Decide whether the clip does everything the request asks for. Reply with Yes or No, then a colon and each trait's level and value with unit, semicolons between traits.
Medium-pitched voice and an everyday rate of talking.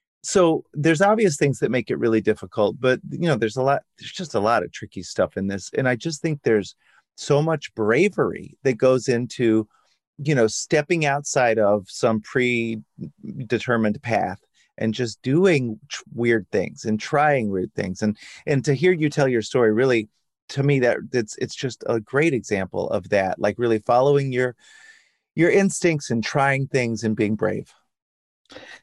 No: low, 130 Hz; average, 175 wpm